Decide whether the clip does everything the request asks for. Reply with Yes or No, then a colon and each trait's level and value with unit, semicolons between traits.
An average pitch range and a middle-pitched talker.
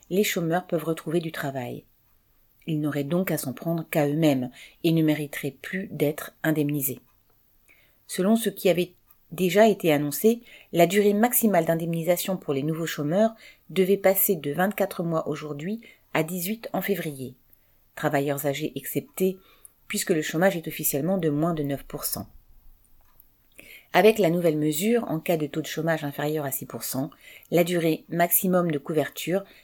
Yes: average, 4.2 semitones; medium, 165 Hz